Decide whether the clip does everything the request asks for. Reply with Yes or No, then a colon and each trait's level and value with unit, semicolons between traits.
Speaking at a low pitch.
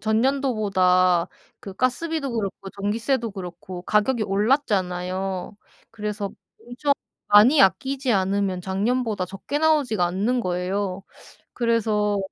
No: high, 210 Hz